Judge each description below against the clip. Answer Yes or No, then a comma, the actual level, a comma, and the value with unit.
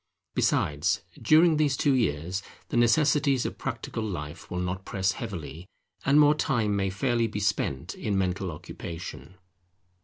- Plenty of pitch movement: Yes, wide, 6.6 semitones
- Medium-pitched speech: No, low, 100 Hz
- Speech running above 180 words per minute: No, average, 145 wpm